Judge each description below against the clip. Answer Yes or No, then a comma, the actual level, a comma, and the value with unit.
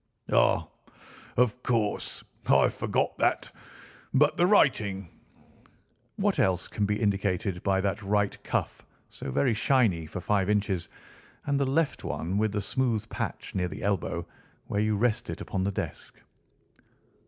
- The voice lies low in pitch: Yes, low, 105 Hz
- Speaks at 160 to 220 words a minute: No, average, 145 wpm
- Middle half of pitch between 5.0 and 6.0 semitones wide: No, average, 3.8 semitones